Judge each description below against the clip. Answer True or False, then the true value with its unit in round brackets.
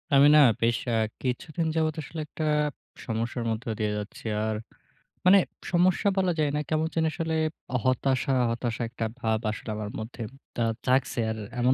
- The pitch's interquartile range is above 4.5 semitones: True (5.5 semitones)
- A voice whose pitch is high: False (130 Hz)